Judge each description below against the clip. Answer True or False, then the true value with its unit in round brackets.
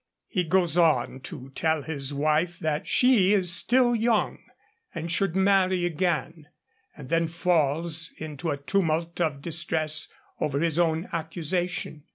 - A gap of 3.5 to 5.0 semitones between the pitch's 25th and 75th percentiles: False (2.7 semitones)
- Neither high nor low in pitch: True (165 Hz)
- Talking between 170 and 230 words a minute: False (140 wpm)